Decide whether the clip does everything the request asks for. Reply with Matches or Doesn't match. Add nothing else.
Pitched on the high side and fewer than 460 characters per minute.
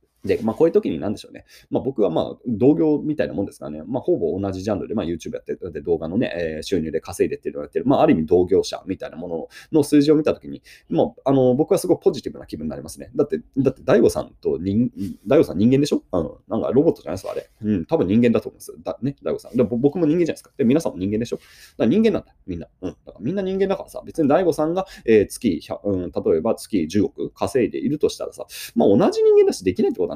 Doesn't match